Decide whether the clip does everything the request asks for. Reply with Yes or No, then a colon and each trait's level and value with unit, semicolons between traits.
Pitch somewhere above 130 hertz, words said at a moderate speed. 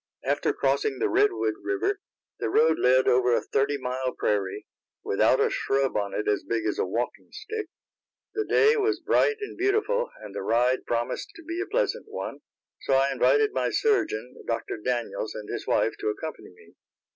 Yes: medium, 140 Hz; average, 180 wpm